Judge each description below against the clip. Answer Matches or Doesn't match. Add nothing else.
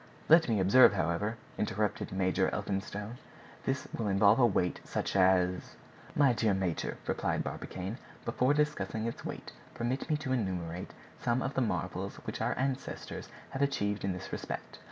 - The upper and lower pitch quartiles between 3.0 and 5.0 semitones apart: Doesn't match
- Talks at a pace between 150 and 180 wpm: Matches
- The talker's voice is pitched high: Doesn't match